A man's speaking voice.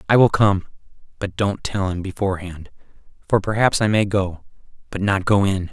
Yes: male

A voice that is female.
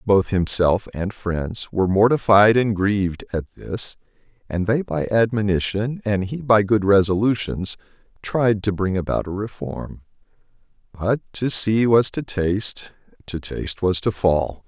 No: male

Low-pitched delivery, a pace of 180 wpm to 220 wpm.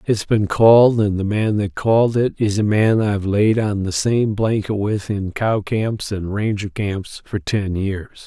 Yes: low, 105 Hz; fast, 205 wpm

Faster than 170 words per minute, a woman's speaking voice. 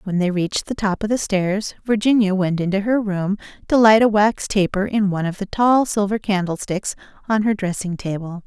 Yes: fast, 205 wpm; female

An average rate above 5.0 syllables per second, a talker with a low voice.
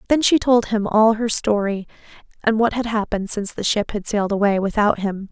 No: 5.7 syllables/s; high, 215 Hz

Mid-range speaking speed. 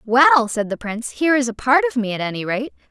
No: fast, 270 wpm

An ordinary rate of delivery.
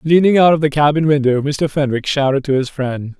No: fast, 225 wpm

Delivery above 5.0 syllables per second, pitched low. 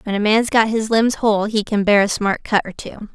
No: 5.3 syllables/s; high, 210 Hz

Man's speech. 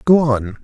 Yes: male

